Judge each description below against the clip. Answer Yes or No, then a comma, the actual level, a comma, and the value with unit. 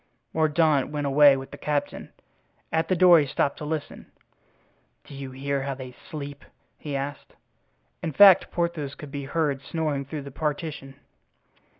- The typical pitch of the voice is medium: Yes, medium, 145 Hz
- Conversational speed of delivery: Yes, average, 160 wpm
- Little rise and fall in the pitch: Yes, narrow, 2.3 semitones